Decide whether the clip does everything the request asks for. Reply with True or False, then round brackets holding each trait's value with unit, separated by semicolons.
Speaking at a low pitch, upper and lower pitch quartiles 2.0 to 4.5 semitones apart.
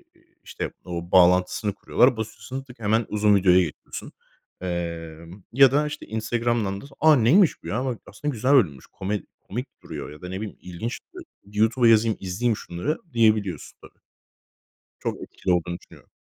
False (105 Hz; 4.9 semitones)